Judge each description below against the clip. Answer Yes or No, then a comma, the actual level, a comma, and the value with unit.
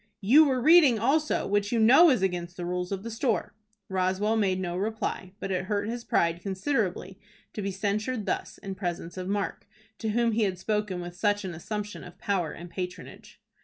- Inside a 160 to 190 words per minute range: No, average, 200 wpm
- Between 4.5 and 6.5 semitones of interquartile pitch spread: No, average, 3.3 semitones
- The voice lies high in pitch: Yes, high, 200 Hz